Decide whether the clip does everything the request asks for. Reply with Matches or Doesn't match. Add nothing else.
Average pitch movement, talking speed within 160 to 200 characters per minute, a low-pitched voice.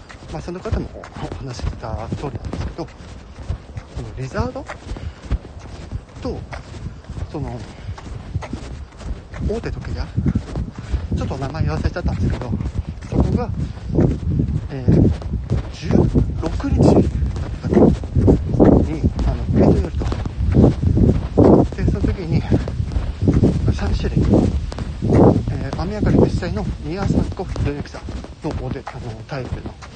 Matches